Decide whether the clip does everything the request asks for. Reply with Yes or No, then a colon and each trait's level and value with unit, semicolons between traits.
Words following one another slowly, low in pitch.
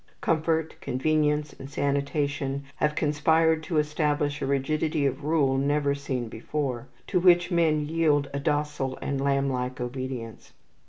No: slow, 130 wpm; medium, 145 Hz